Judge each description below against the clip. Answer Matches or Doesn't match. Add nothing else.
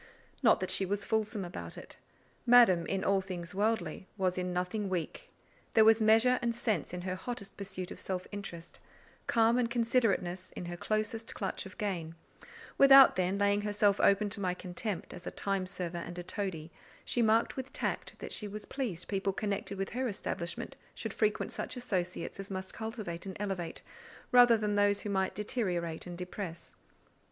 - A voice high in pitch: Matches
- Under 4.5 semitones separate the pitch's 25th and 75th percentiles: Matches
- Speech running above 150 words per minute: Matches